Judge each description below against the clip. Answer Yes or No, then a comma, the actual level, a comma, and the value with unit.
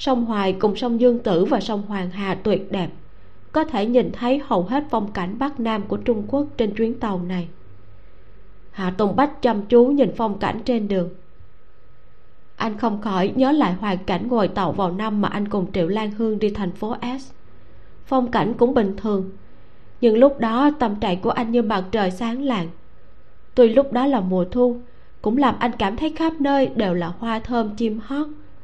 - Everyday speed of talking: Yes, average, 200 wpm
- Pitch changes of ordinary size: Yes, average, 4.6 semitones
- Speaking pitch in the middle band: No, high, 220 Hz